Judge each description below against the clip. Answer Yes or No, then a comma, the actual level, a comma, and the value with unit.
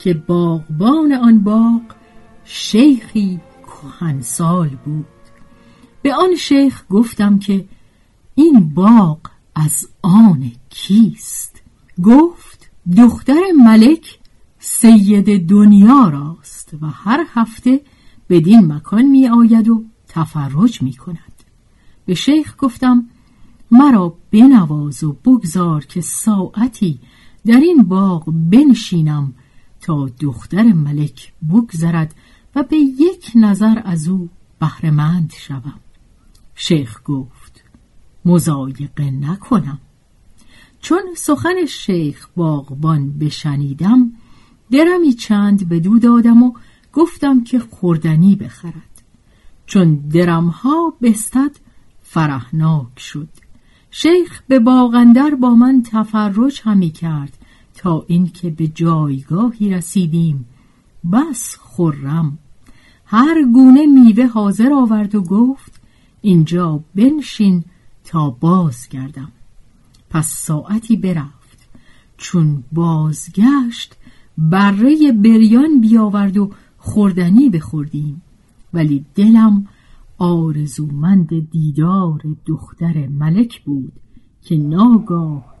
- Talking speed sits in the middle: No, slow, 95 wpm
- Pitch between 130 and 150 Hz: No, medium, 180 Hz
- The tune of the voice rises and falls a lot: Yes, wide, 7.3 semitones